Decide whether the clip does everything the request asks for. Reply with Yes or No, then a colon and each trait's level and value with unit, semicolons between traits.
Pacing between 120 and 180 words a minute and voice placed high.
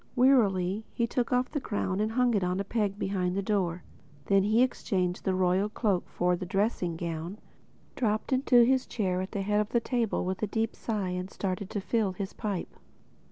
No: fast, 205 wpm; high, 200 Hz